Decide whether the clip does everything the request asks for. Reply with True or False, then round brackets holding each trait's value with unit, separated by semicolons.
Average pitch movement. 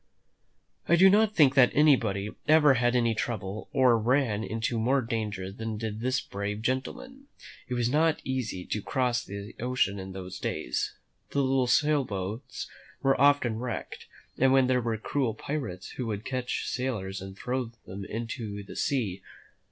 True (4.2 semitones)